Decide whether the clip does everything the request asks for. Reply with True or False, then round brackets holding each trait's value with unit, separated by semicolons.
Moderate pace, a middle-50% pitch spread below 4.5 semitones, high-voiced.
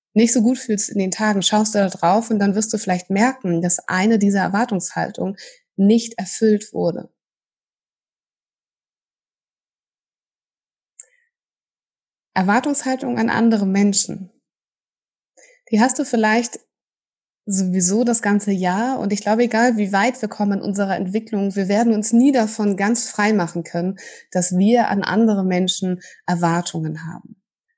True (135 wpm; 3.4 semitones; 210 Hz)